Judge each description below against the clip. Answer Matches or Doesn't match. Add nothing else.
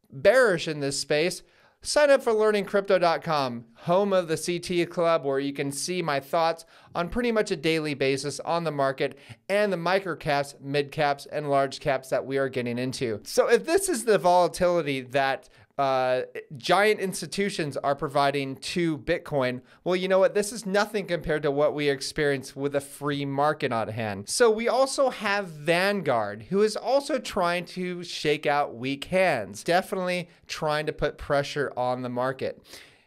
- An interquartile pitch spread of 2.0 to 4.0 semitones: Doesn't match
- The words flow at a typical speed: Matches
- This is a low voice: Doesn't match